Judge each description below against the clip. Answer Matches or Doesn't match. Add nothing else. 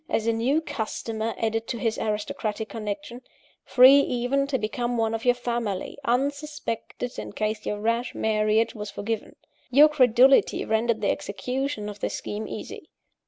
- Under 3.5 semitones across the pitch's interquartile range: Matches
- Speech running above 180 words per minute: Doesn't match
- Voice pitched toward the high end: Matches